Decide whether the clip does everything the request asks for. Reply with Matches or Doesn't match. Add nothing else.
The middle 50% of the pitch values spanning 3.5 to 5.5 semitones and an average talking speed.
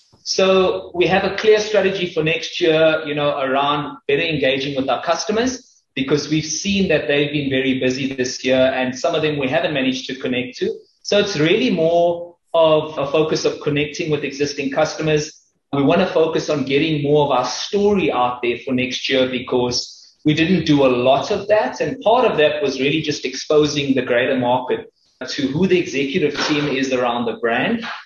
Matches